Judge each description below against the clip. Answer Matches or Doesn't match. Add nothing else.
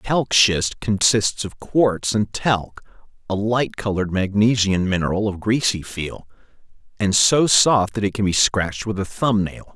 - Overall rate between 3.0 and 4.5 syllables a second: Matches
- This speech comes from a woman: Doesn't match